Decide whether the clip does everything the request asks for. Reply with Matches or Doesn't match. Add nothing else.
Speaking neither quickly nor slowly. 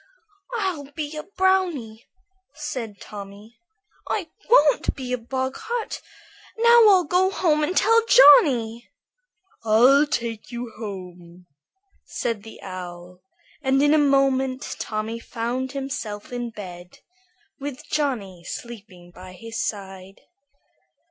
Doesn't match